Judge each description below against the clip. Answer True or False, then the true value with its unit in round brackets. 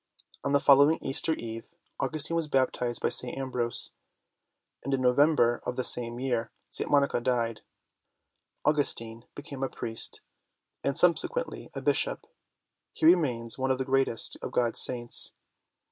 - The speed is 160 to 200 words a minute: False (145 wpm)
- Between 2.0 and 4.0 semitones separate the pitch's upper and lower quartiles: True (3.1 semitones)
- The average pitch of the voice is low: True (130 Hz)